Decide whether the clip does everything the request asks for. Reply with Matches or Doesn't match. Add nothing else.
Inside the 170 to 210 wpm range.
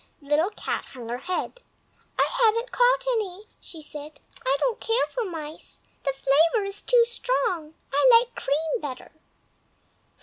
Doesn't match